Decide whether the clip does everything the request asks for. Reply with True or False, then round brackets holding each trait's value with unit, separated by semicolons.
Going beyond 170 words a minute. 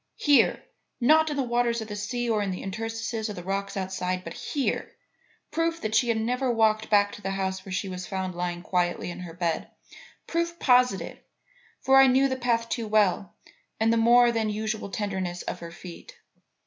True (200 wpm)